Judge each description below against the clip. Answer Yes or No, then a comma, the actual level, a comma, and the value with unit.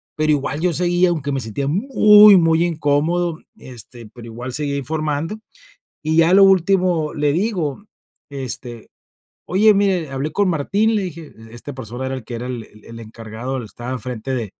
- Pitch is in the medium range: Yes, medium, 150 Hz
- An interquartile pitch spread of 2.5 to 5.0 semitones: No, wide, 5.6 semitones